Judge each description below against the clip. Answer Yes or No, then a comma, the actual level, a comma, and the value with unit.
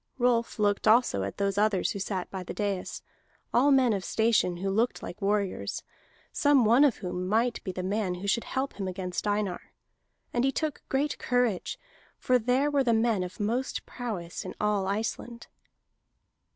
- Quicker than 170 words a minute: Yes, average, 180 wpm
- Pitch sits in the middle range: No, high, 215 Hz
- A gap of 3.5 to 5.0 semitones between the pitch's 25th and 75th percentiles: Yes, average, 4.2 semitones